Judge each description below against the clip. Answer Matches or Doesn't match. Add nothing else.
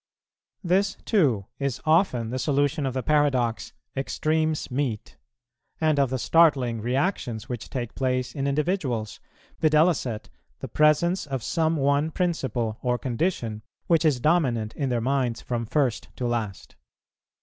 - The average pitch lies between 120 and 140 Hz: Matches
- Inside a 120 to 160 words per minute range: Matches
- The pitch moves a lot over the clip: Doesn't match